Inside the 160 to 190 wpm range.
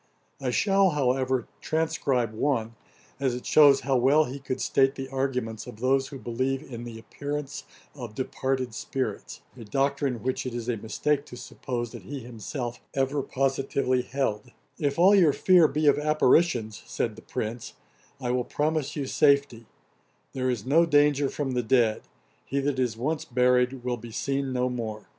Yes: average, 170 wpm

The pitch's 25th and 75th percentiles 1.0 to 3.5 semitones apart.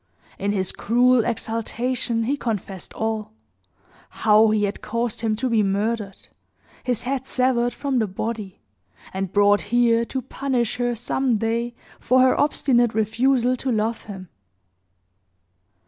Yes: narrow, 2.6 semitones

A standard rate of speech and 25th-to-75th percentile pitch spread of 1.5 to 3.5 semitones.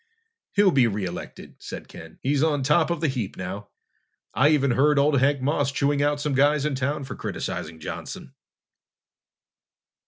Yes: average, 165 wpm; narrow, 2.5 semitones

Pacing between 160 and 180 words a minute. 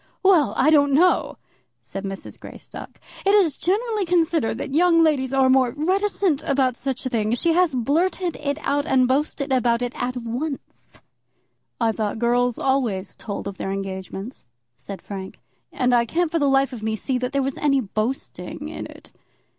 Yes: average, 175 wpm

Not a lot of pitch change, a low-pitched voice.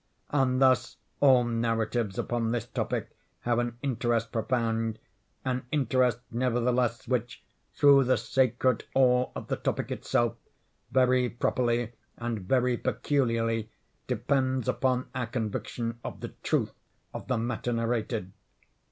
Yes: narrow, 1.9 semitones; low, 120 Hz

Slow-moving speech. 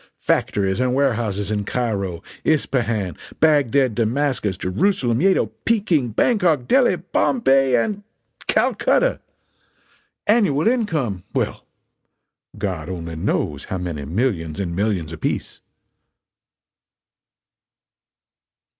Yes: slow, 90 wpm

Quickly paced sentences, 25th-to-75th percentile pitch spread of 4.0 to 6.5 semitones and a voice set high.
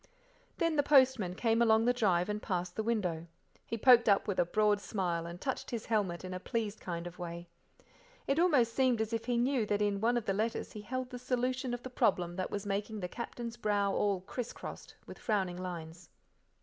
Yes: fast, 215 wpm; average, 4.7 semitones; high, 215 Hz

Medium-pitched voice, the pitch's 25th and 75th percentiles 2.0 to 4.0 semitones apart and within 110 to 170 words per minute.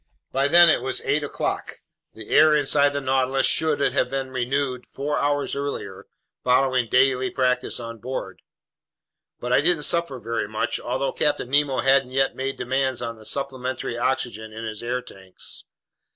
No: low, 130 Hz; narrow, 2.4 semitones; average, 165 wpm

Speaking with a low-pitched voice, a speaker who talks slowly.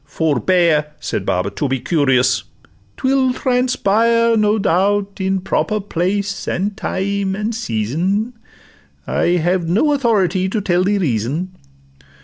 No: high, 190 Hz; slow, 125 wpm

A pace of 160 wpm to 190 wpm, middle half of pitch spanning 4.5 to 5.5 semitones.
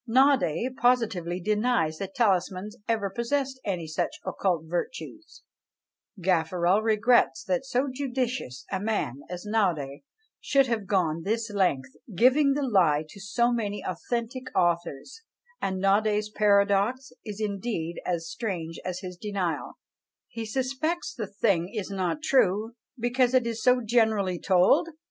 No: slow, 135 wpm; average, 5.2 semitones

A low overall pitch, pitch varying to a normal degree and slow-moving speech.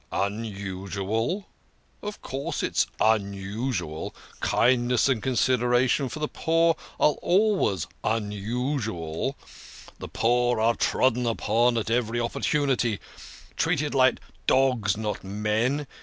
Yes: low, 115 Hz; average, 3.9 semitones; slow, 110 wpm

